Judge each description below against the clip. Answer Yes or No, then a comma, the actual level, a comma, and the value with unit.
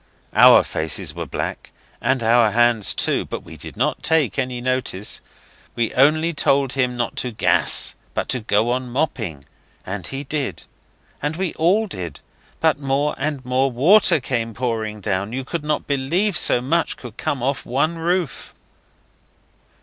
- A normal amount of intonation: Yes, average, 4.3 semitones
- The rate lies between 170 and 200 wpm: No, average, 160 wpm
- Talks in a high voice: No, low, 130 Hz